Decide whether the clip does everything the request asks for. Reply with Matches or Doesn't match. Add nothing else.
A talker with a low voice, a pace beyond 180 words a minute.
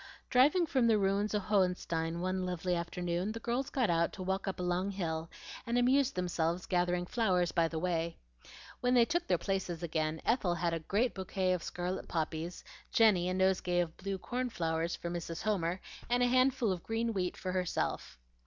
Doesn't match